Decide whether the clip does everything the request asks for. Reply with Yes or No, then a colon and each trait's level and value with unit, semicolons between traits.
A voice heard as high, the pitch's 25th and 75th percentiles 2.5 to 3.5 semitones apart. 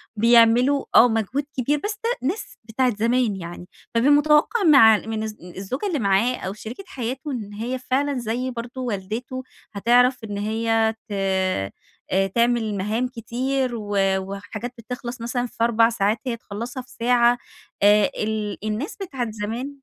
Yes: high, 235 Hz; average, 3.1 semitones